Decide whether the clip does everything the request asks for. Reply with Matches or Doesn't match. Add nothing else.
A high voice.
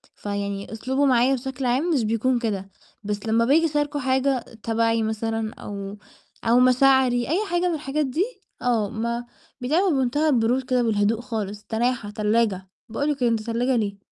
Matches